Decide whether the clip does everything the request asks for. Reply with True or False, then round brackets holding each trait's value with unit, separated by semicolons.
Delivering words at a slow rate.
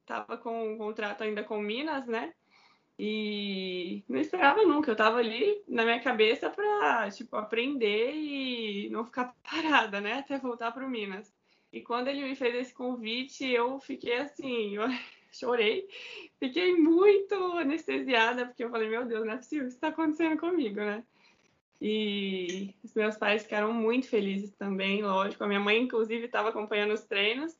False (165 wpm)